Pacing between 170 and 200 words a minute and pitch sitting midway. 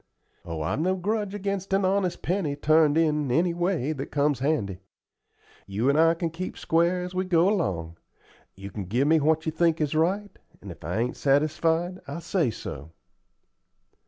Yes: average, 180 wpm; medium, 160 Hz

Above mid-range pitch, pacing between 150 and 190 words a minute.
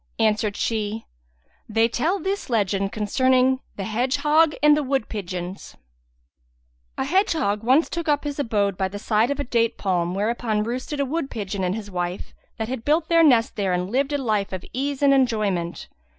Yes: high, 225 Hz; average, 180 wpm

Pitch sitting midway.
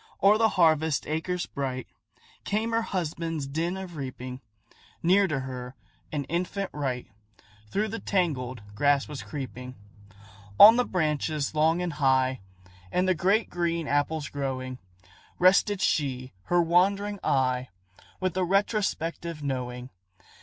Yes: medium, 160 Hz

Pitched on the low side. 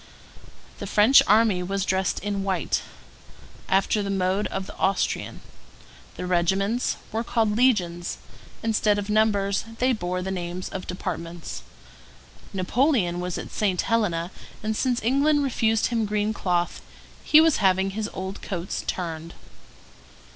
No: high, 195 Hz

